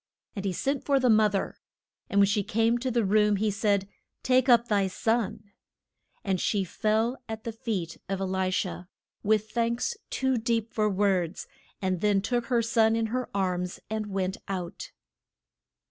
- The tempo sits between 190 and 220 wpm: No, average, 175 wpm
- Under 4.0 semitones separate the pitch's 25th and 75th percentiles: Yes, average, 3.1 semitones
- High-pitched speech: Yes, high, 215 Hz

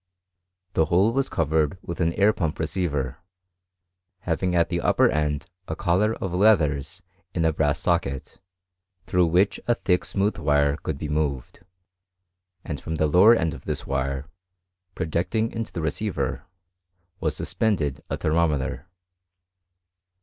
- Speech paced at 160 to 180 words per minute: No, average, 140 wpm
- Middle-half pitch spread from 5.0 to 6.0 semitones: No, average, 4.0 semitones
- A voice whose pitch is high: No, very low, 80 Hz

